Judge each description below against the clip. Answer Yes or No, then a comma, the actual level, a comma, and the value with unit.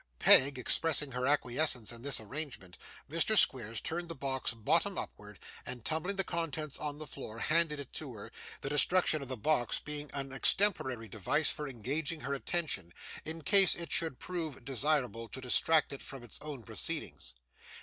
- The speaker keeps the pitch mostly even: No, average, 4.2 semitones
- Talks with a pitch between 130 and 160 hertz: Yes, medium, 140 Hz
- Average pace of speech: Yes, average, 170 wpm